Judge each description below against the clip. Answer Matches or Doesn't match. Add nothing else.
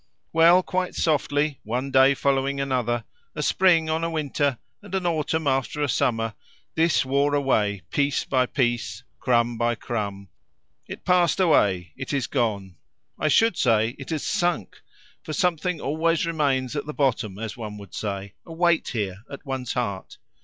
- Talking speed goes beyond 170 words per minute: Doesn't match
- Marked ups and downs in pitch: Matches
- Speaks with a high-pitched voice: Doesn't match